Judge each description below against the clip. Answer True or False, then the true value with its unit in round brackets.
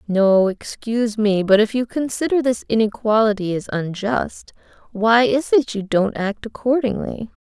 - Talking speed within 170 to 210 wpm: False (145 wpm)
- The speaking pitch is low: False (220 Hz)